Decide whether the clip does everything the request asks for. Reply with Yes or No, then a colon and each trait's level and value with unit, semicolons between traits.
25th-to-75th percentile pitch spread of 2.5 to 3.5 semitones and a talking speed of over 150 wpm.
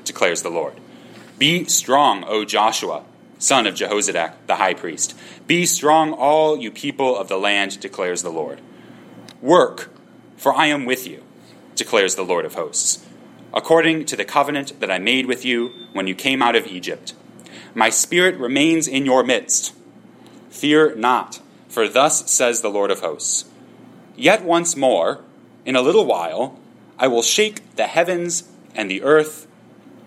No: average, 4.7 semitones; average, 160 wpm